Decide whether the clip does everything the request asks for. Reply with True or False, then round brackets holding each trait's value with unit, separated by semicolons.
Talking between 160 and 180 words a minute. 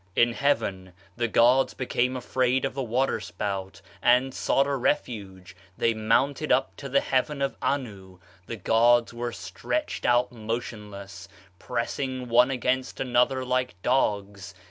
False (140 wpm)